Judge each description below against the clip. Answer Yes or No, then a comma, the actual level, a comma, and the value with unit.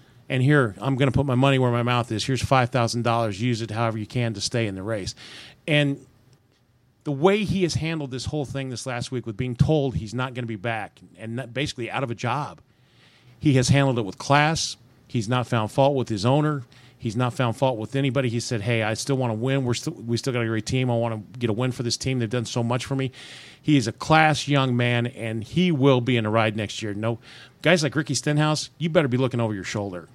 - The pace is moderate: No, fast, 260 wpm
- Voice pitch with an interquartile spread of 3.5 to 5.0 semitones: No, average, 2.8 semitones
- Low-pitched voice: Yes, low, 125 Hz